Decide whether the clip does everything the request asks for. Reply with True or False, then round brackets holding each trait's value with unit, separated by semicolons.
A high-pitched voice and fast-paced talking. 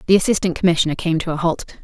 False (170 Hz; 230 wpm)